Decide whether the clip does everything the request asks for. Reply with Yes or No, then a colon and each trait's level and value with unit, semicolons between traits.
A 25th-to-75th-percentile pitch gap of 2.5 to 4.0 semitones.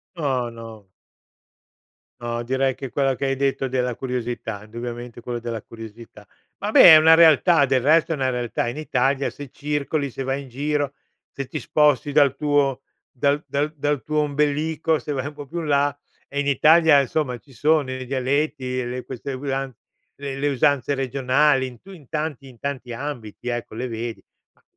Yes: average, 2.9 semitones